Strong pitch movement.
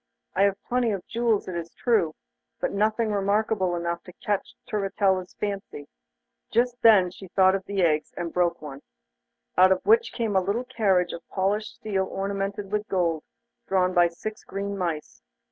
No: average, 2.8 semitones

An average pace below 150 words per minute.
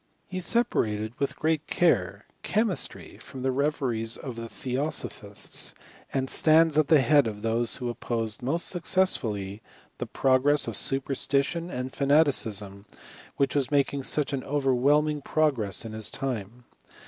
Yes: average, 140 wpm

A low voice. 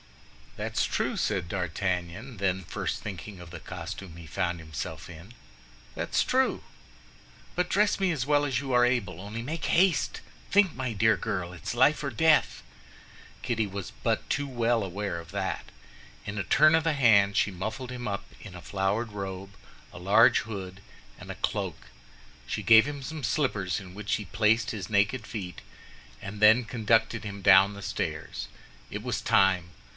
Yes: low, 105 Hz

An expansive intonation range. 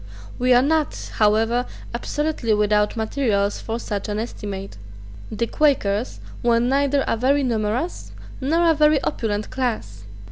No: average, 4.8 semitones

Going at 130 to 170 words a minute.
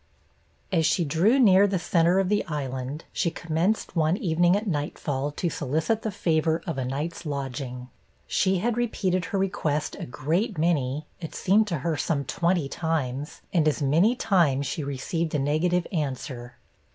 Yes: average, 165 wpm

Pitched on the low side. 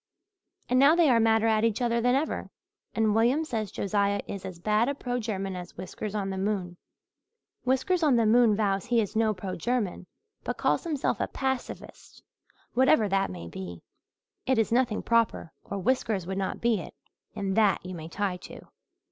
No: high, 215 Hz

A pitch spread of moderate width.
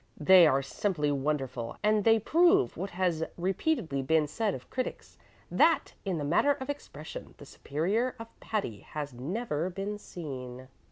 No: wide, 7.1 semitones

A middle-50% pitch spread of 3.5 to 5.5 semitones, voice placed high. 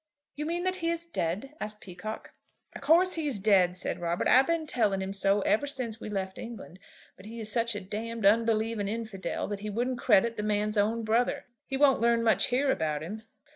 Yes: average, 3.9 semitones; high, 220 Hz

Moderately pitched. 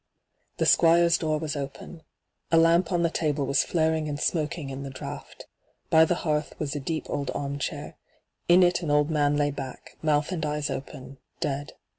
Yes: medium, 150 Hz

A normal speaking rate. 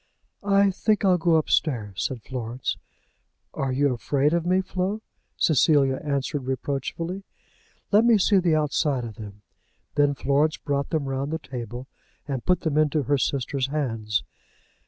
Yes: average, 150 wpm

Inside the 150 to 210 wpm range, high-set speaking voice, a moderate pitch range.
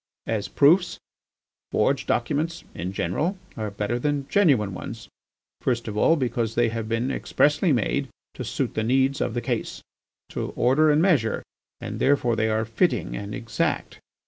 No: average, 160 wpm; low, 120 Hz; average, 4.6 semitones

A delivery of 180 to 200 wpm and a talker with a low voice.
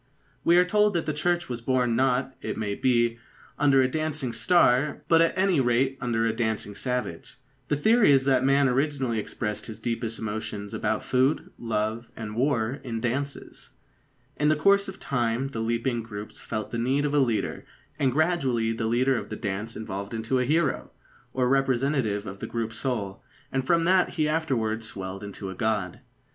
Yes: average, 185 wpm; low, 125 Hz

